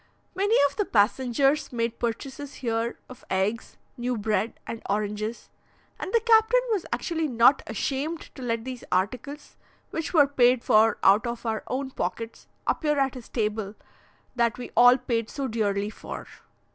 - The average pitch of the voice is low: No, high, 240 Hz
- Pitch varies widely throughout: No, average, 3.9 semitones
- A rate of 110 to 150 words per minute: No, average, 160 wpm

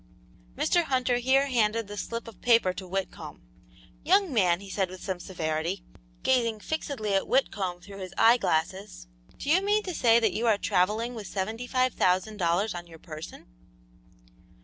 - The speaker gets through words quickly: No, average, 170 wpm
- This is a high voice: Yes, high, 215 Hz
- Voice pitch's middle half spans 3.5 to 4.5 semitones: No, average, 4.9 semitones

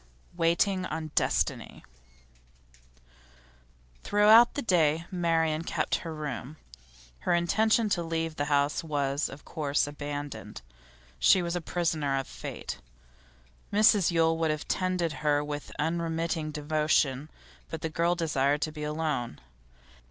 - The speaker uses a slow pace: Yes, slow, 125 wpm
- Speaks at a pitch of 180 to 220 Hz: No, medium, 160 Hz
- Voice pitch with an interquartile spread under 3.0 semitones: Yes, narrow, 2.6 semitones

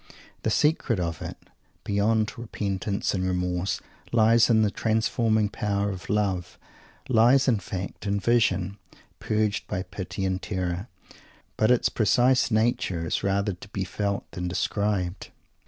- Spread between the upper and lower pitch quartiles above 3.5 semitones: No, average, 2.9 semitones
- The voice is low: Yes, low, 100 Hz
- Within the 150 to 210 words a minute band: No, average, 140 wpm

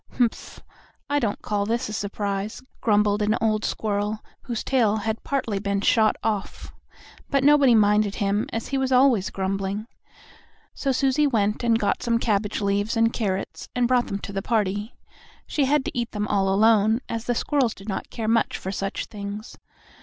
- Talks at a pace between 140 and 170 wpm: No, average, 180 wpm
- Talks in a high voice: Yes, high, 215 Hz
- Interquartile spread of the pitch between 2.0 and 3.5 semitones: Yes, average, 2.8 semitones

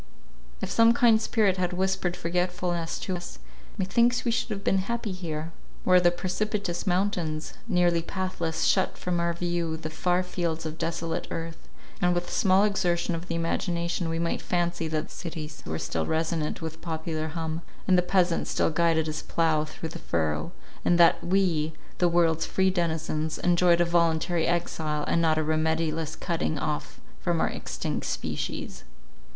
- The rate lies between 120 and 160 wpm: No, average, 170 wpm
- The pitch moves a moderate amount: No, narrow, 2.1 semitones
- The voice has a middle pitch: Yes, medium, 170 Hz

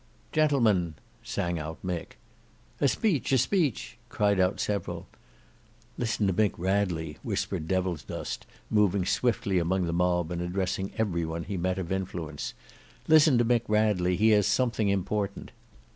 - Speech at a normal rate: Yes, average, 145 wpm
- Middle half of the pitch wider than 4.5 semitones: No, average, 3.8 semitones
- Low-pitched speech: Yes, very low, 95 Hz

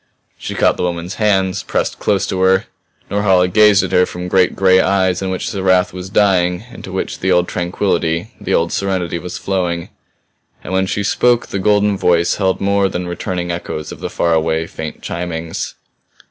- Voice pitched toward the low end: Yes, very low, 95 Hz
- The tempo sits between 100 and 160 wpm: No, average, 190 wpm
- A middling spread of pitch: No, narrow, 1.9 semitones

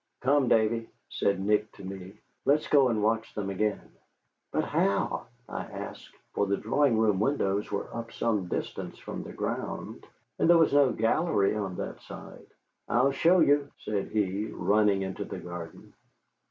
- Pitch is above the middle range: No, low, 110 Hz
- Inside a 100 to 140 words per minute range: No, average, 165 wpm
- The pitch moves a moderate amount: Yes, average, 4.6 semitones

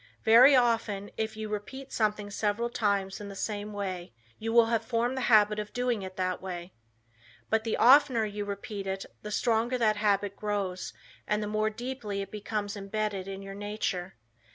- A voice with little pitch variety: Yes, narrow, 2.1 semitones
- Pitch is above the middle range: Yes, high, 210 Hz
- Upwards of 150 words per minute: Yes, average, 180 wpm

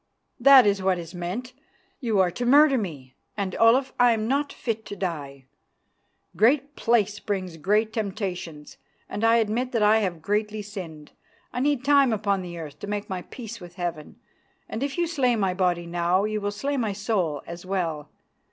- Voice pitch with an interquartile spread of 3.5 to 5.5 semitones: Yes, average, 5.0 semitones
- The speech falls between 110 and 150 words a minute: No, average, 180 wpm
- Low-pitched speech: No, high, 205 Hz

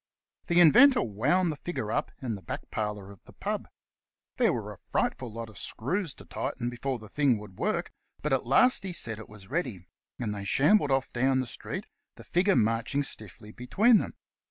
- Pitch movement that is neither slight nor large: No, wide, 6.9 semitones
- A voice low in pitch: Yes, low, 125 Hz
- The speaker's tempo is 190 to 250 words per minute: Yes, average, 200 wpm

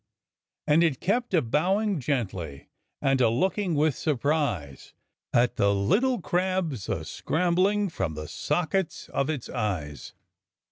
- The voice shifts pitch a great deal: Yes, wide, 8.4 semitones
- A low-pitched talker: No, medium, 150 Hz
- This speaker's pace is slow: Yes, slow, 130 wpm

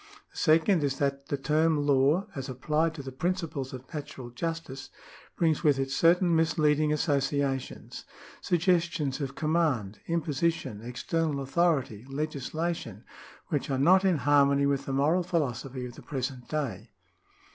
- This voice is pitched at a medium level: Yes, medium, 145 Hz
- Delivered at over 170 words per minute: No, average, 145 wpm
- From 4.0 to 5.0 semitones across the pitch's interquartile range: No, average, 3.4 semitones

